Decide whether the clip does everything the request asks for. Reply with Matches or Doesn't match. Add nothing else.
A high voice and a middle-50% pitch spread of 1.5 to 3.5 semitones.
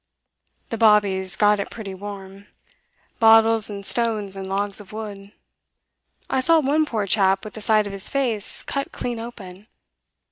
Matches